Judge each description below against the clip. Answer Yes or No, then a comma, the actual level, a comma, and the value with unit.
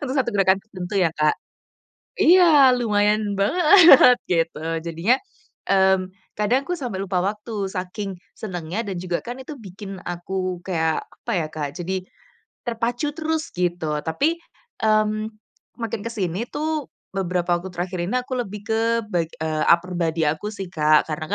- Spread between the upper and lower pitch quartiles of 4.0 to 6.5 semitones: Yes, average, 4.7 semitones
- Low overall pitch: No, high, 195 Hz